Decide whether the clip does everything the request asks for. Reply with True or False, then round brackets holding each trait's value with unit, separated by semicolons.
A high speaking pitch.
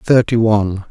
False (110 Hz)